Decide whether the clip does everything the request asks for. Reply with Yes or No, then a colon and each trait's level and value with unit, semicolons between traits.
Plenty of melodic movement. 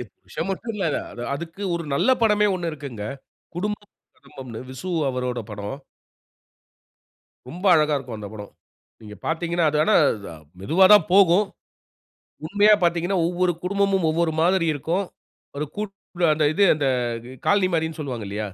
Yes: wide, 5.8 semitones